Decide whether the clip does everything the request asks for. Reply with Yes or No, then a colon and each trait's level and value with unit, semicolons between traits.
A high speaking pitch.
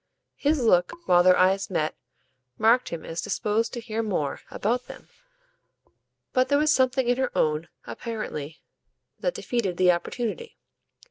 Yes: high, 220 Hz